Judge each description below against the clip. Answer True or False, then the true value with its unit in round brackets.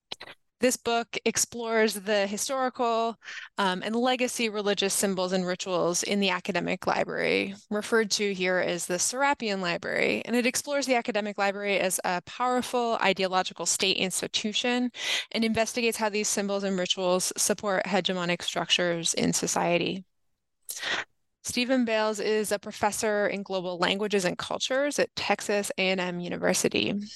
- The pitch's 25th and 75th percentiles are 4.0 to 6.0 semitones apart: False (3.5 semitones)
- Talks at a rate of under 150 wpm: True (135 wpm)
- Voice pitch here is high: True (205 Hz)